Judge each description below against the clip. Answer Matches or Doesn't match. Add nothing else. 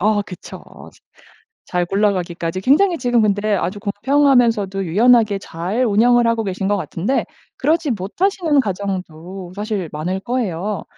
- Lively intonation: Doesn't match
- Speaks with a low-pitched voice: Doesn't match